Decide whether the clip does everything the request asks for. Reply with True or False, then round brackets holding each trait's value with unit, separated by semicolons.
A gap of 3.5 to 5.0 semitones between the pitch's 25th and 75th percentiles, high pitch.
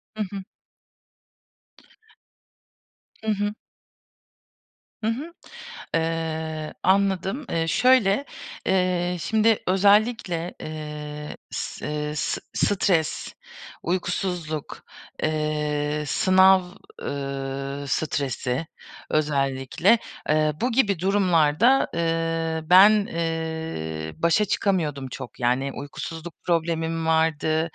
False (4.1 semitones; 165 Hz)